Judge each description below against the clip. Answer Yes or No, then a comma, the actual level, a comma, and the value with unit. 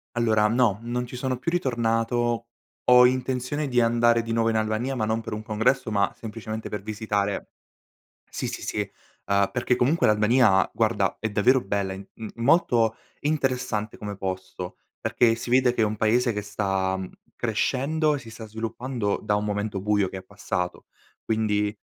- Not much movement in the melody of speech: No, average, 3.0 semitones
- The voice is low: Yes, low, 115 Hz